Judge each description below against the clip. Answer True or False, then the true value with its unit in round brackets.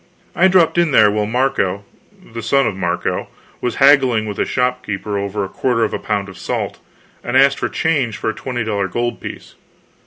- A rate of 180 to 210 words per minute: True (195 wpm)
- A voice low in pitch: True (115 Hz)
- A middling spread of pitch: True (4.7 semitones)